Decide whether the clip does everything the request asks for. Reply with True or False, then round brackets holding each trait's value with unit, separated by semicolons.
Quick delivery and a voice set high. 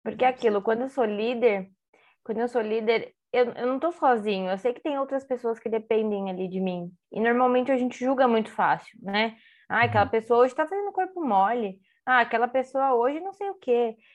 True (215 wpm; 240 Hz)